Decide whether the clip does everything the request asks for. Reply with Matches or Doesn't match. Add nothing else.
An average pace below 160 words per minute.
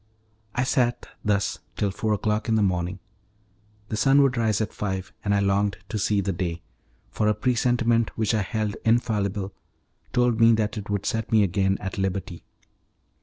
Doesn't match